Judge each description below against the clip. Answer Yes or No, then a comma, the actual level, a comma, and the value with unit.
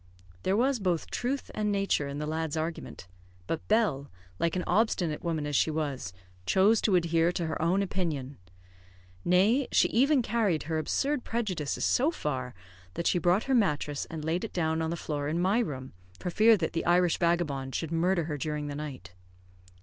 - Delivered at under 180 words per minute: No, average, 190 wpm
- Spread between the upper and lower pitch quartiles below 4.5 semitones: No, average, 4.8 semitones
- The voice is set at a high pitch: No, medium, 170 Hz